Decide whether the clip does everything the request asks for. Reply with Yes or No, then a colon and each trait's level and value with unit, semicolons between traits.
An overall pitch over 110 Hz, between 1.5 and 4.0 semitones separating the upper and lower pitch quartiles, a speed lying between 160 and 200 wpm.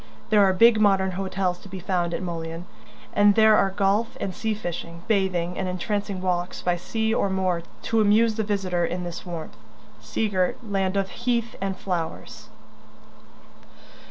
Yes: high, 190 Hz; narrow, 2.6 semitones; average, 165 wpm